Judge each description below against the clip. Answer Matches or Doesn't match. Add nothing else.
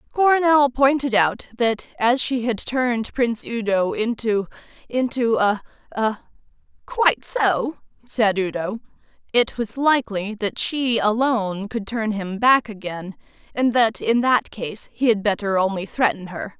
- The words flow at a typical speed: Doesn't match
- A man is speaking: Doesn't match